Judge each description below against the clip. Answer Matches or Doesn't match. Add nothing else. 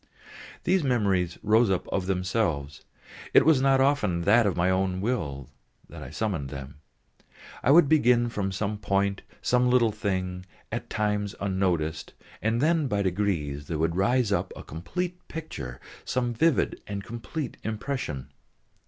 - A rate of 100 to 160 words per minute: Matches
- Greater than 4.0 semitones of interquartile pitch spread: Matches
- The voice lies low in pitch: Matches